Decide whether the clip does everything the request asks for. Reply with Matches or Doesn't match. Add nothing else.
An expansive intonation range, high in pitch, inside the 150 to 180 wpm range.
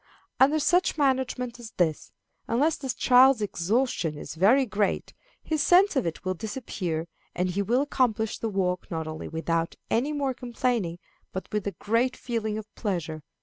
Matches